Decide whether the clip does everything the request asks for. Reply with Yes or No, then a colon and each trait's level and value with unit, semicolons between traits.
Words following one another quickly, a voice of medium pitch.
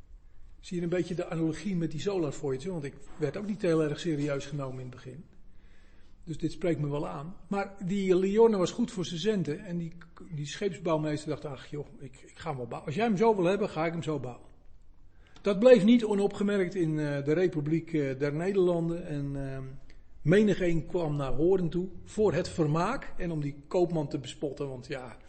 Yes: fast, 210 wpm; medium, 160 Hz